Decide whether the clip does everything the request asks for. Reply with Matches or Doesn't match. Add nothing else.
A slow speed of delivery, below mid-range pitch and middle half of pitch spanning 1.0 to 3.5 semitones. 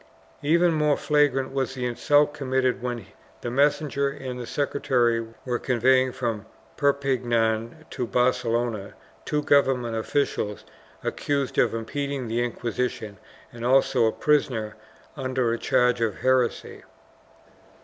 Matches